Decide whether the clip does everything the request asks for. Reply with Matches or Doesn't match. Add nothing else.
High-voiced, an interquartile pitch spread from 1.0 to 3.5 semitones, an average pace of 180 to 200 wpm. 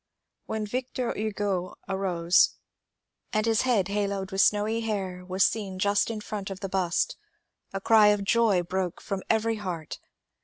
Doesn't match